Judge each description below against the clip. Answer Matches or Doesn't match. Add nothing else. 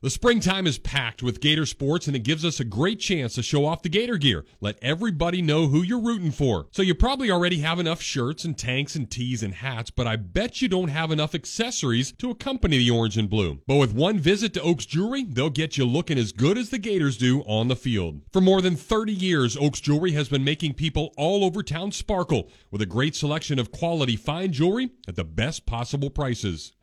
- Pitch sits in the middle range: Matches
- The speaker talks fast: Matches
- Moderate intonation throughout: Doesn't match